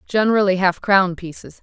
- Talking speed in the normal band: Yes, average, 150 wpm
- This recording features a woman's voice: Yes, female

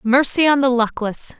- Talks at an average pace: Yes, average, 175 wpm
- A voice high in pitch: Yes, very high, 250 Hz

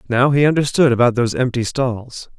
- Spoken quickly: No, average, 175 wpm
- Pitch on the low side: Yes, low, 125 Hz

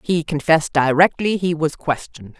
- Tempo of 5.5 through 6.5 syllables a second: No, 5.3 syllables/s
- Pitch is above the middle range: No, medium, 160 Hz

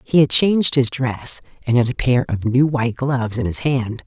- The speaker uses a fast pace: Yes, fast, 235 wpm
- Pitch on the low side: Yes, low, 130 Hz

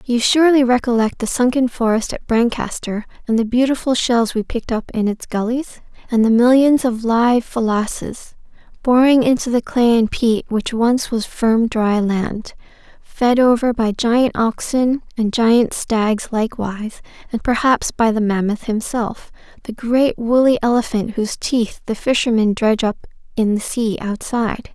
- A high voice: Yes, high, 235 Hz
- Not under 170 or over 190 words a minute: No, average, 160 wpm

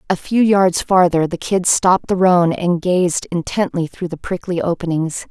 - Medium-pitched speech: Yes, medium, 180 Hz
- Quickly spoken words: No, average, 180 wpm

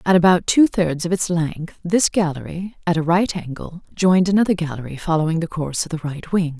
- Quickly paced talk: Yes, fast, 210 wpm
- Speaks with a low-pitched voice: No, medium, 170 Hz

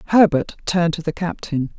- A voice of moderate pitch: Yes, medium, 170 Hz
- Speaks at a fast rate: No, average, 170 wpm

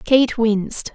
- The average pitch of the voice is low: No, high, 230 Hz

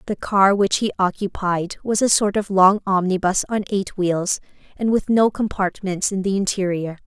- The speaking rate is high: No, average, 180 wpm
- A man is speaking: No, female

